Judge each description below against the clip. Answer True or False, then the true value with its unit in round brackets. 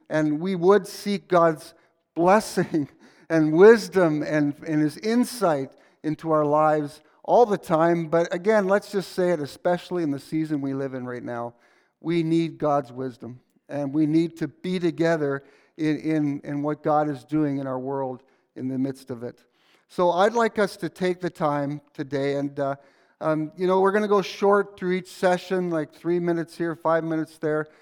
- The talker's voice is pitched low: False (160 Hz)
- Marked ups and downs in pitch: False (3.8 semitones)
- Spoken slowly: False (190 wpm)